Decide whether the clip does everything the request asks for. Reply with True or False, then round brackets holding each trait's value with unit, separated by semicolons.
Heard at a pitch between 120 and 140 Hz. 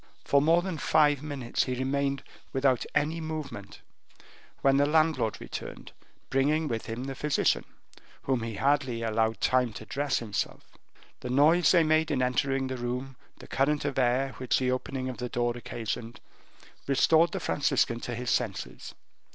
True (135 Hz)